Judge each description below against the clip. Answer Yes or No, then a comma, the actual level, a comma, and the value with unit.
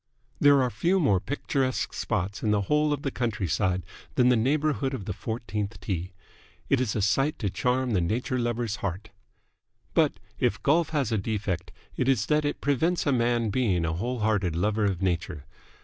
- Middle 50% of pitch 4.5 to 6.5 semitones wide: Yes, average, 5.2 semitones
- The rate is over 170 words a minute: Yes, average, 185 wpm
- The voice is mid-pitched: No, low, 115 Hz